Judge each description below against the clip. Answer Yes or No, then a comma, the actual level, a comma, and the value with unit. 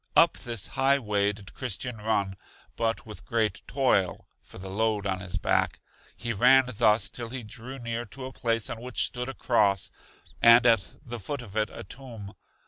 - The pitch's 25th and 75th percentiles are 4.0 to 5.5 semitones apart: No, average, 3.4 semitones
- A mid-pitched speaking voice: No, low, 115 Hz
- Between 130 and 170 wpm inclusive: No, average, 190 wpm